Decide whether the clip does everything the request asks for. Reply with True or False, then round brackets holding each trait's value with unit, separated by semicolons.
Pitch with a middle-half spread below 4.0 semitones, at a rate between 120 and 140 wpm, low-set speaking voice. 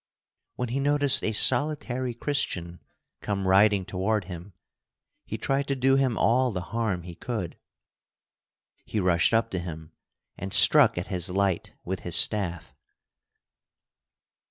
False (5.6 semitones; 135 wpm; 105 Hz)